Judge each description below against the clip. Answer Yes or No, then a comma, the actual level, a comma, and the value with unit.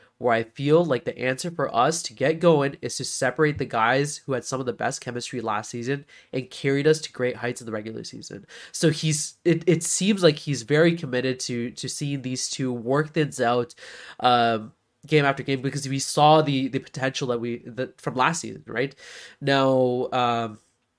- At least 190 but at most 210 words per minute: Yes, fast, 205 wpm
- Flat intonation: No, average, 3.6 semitones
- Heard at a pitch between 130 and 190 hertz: Yes, low, 135 Hz